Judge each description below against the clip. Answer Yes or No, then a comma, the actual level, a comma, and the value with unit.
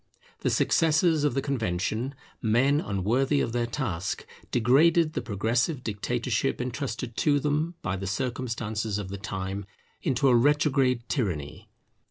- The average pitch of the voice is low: Yes, low, 120 Hz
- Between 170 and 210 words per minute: No, slow, 135 wpm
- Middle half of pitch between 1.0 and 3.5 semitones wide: No, average, 5.2 semitones